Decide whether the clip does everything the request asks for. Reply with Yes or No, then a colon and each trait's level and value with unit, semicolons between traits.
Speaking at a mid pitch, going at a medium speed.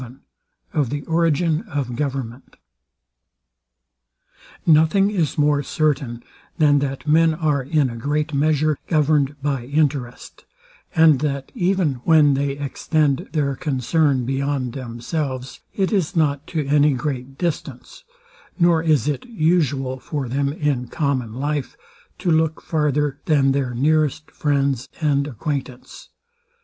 No: medium, 145 Hz; slow, 125 wpm